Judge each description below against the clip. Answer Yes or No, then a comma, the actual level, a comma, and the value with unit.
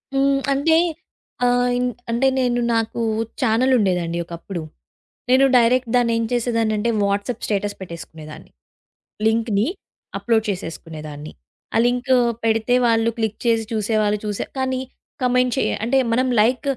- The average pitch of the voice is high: Yes, high, 230 Hz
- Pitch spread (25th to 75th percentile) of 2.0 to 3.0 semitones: No, average, 3.4 semitones